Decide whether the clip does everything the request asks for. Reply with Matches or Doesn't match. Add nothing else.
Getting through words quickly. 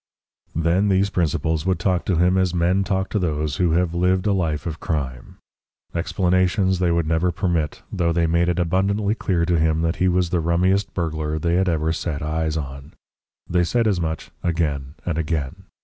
Doesn't match